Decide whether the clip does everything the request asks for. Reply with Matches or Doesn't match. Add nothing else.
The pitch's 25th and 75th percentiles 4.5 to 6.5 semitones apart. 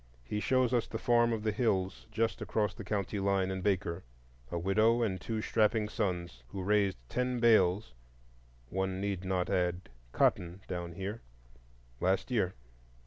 Doesn't match